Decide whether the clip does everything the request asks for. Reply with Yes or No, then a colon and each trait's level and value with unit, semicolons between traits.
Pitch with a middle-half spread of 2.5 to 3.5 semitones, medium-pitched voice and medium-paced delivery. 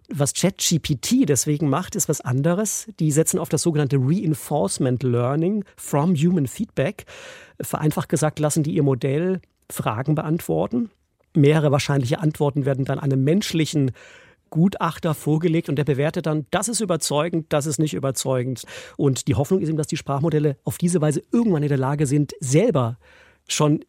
Yes: average, 3.2 semitones; medium, 155 Hz; average, 160 wpm